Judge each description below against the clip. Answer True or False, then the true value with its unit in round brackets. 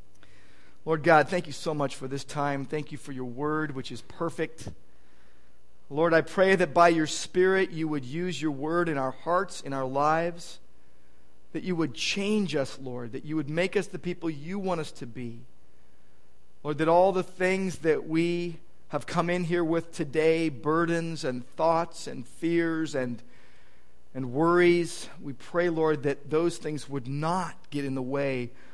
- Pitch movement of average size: True (4.5 semitones)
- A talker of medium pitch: True (155 Hz)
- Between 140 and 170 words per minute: False (180 wpm)